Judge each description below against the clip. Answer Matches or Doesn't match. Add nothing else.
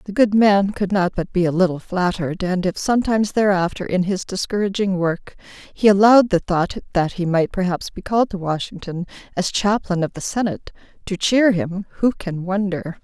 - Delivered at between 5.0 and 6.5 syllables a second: Matches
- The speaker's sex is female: Matches